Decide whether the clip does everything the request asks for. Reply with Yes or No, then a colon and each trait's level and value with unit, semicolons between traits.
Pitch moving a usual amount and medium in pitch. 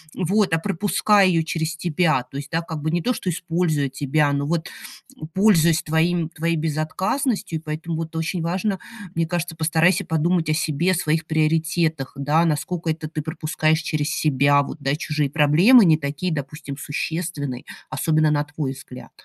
No: narrow, 2.2 semitones; medium, 160 Hz